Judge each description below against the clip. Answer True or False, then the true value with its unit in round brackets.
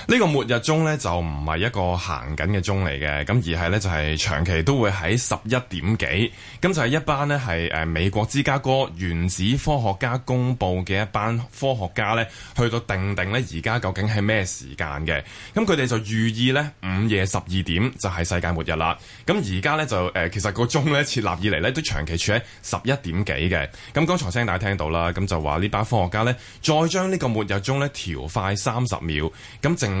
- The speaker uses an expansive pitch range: True (5.9 semitones)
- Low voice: True (105 Hz)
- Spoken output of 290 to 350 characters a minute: True (310 characters per minute)